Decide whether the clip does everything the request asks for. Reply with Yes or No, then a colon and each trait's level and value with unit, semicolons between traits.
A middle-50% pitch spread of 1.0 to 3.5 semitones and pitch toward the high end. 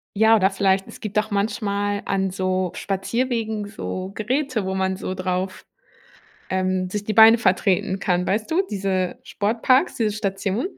Yes: narrow, 2.6 semitones; high, 200 Hz